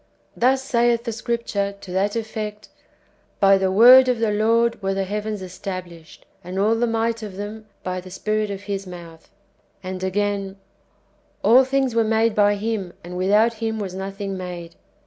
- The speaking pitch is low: No, high, 205 Hz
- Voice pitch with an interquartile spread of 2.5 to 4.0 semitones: Yes, average, 3.0 semitones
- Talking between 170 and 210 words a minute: Yes, average, 180 wpm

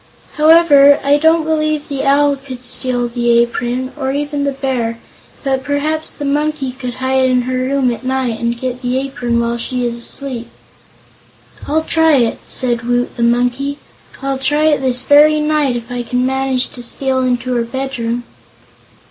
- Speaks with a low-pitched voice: No, very high, 260 Hz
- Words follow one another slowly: No, average, 175 wpm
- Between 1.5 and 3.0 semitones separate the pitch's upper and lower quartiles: Yes, average, 2.7 semitones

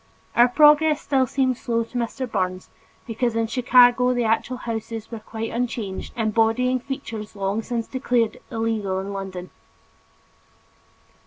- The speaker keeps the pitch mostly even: Yes, narrow, 2.3 semitones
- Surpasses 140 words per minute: No, slow, 135 wpm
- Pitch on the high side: Yes, high, 230 Hz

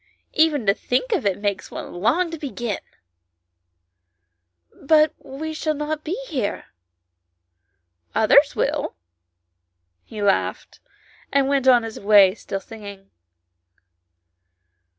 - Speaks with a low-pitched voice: No, high, 215 Hz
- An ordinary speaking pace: No, slow, 115 wpm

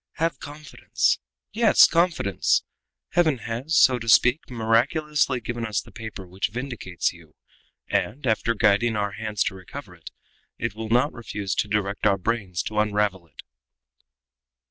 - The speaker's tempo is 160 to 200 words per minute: No, average, 145 wpm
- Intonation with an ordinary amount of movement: Yes, average, 4.0 semitones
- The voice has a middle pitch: No, low, 110 Hz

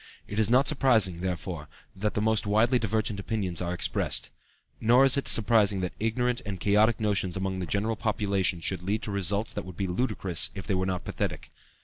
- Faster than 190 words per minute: Yes, average, 200 wpm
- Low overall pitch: Yes, low, 100 Hz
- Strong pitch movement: No, average, 2.9 semitones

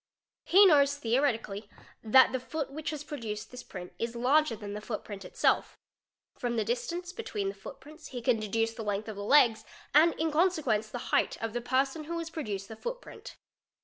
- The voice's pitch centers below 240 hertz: No, high, 245 Hz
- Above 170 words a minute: Yes, average, 190 wpm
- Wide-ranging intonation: Yes, wide, 5.7 semitones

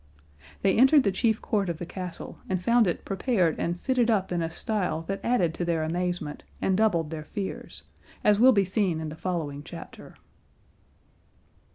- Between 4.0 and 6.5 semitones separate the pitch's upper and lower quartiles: Yes, average, 4.4 semitones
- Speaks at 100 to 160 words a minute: No, average, 180 wpm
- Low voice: No, medium, 185 Hz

